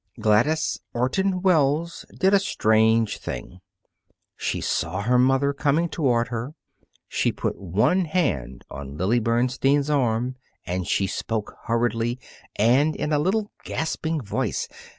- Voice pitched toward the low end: Yes, low, 125 Hz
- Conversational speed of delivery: No, slow, 130 wpm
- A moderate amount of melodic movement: No, wide, 5.7 semitones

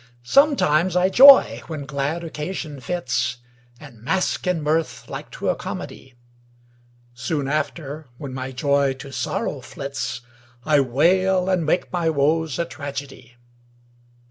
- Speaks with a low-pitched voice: No, medium, 150 Hz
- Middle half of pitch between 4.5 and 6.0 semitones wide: No, average, 3.9 semitones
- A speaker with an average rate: No, slow, 130 wpm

